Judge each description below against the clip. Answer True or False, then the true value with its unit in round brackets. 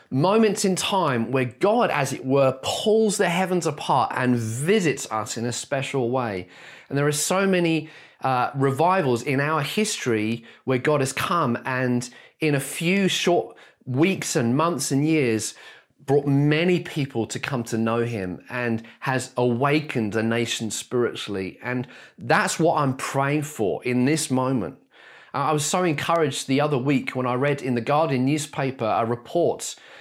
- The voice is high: False (135 Hz)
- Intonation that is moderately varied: True (4.4 semitones)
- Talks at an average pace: True (165 wpm)